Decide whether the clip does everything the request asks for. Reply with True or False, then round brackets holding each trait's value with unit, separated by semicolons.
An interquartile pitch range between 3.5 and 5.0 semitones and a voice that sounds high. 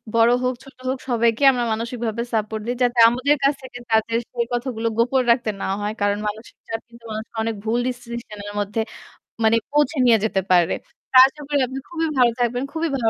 False (2.4 semitones; 235 Hz)